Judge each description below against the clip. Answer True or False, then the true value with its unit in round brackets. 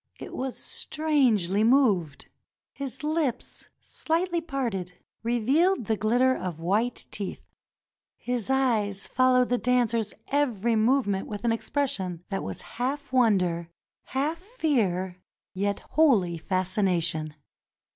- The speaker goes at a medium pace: False (110 wpm)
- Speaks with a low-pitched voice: False (235 Hz)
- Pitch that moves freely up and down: True (5.9 semitones)